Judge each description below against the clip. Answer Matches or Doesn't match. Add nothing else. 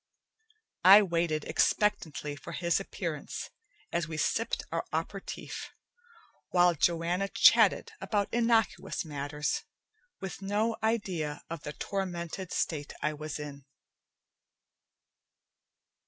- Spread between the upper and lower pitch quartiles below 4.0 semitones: Doesn't match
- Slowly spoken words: Matches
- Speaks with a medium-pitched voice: Matches